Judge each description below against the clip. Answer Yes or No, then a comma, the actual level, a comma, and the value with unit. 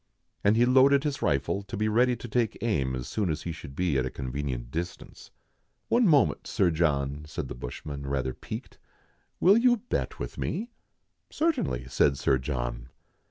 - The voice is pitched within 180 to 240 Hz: No, very low, 85 Hz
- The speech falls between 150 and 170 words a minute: No, average, 190 wpm